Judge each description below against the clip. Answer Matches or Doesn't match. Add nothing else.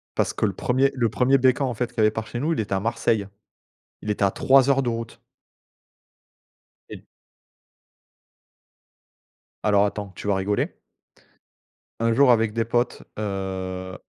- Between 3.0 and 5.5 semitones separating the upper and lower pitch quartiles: Matches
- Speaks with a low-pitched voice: Matches